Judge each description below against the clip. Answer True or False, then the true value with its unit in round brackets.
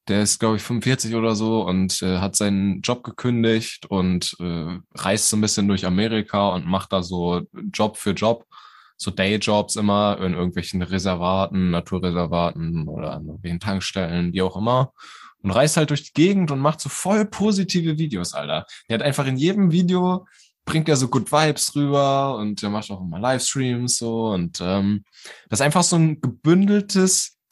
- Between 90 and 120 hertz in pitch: True (110 Hz)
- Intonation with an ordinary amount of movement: False (7.4 semitones)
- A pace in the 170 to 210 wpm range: True (180 wpm)